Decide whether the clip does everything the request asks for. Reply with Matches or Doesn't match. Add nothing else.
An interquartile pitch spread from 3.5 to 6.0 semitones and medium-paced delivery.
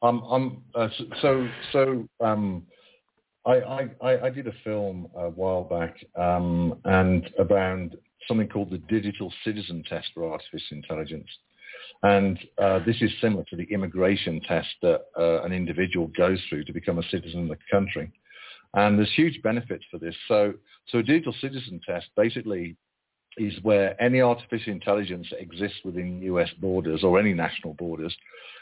Matches